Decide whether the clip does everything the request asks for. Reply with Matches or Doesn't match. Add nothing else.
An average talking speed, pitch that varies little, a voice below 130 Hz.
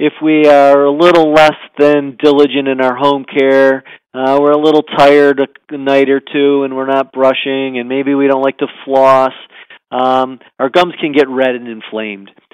Doesn't match